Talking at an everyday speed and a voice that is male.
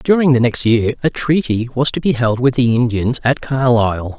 No: fast, 215 wpm; male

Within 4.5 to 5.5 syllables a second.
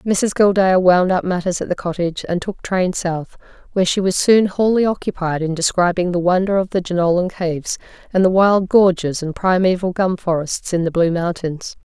Yes: 5.2 syllables/s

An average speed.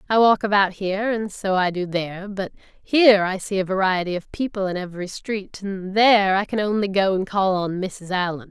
No: fast, 220 wpm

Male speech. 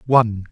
Yes: male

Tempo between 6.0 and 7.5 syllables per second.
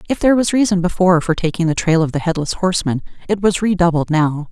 Yes: 6.6 syllables/s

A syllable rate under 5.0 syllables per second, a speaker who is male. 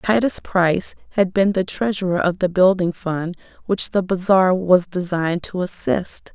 No: 4.5 syllables/s; female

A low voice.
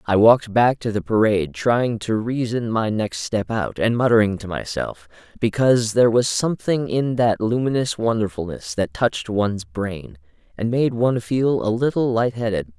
Yes: low, 110 Hz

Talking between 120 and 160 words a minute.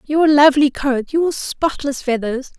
Yes: average, 140 wpm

